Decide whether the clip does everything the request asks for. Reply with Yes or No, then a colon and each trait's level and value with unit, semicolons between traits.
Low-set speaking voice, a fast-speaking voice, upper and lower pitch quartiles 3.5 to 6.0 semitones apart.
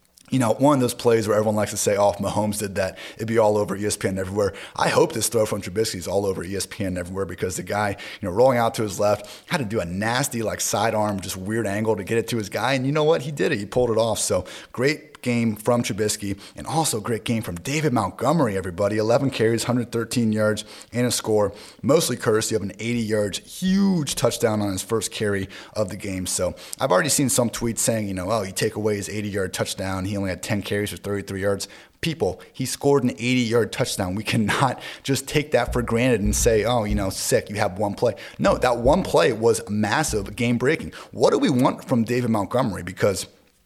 No: low, 110 Hz; fast, 235 wpm; average, 3.0 semitones